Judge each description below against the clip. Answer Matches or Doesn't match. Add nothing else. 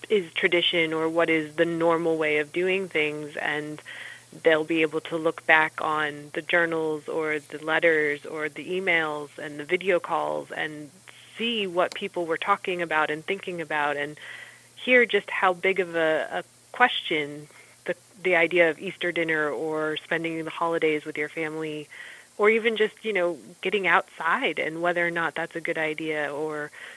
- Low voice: Doesn't match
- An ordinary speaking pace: Matches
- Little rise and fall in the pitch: Matches